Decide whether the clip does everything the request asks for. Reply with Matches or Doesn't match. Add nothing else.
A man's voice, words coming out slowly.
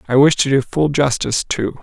Doesn't match